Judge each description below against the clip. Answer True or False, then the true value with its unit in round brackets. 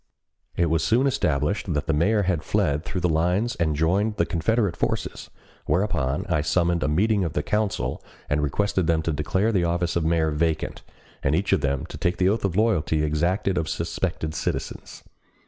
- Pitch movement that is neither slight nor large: True (4.2 semitones)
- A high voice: False (85 Hz)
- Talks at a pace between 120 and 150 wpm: False (190 wpm)